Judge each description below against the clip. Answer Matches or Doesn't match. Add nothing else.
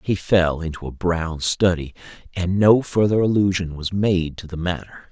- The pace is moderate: Matches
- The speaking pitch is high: Doesn't match